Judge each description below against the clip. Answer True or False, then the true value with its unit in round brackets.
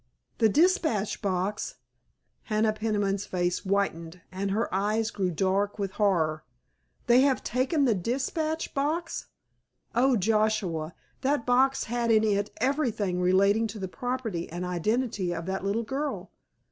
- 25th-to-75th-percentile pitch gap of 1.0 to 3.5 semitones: False (4.7 semitones)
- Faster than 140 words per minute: False (135 wpm)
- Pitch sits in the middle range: False (215 Hz)